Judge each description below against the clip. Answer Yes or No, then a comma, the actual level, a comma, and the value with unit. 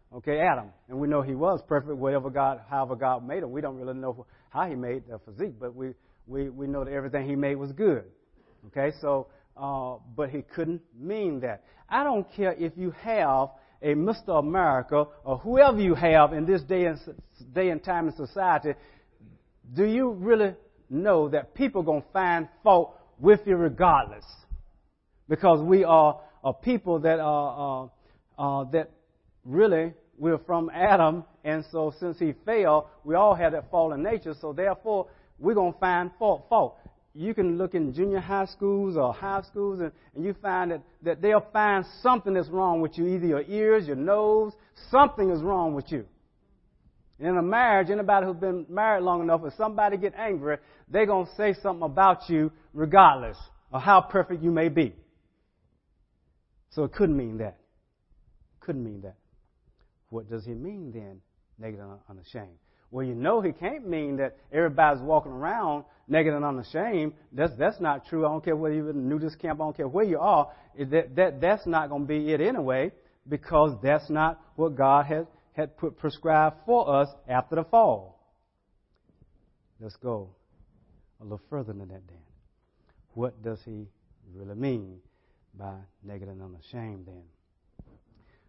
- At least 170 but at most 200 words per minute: Yes, average, 175 wpm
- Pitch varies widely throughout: Yes, wide, 5.8 semitones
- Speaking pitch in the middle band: Yes, medium, 155 Hz